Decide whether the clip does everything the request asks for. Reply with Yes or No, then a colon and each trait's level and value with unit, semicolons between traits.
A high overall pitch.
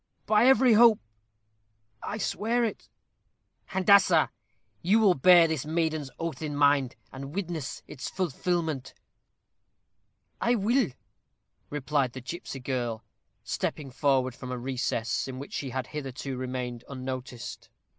No: medium, 145 Hz